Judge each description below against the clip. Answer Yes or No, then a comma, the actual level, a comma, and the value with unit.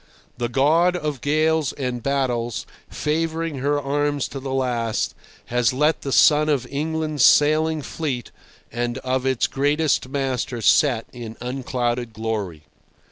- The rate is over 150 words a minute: No, slow, 135 wpm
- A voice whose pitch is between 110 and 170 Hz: Yes, low, 135 Hz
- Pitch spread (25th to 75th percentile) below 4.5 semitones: Yes, average, 3.6 semitones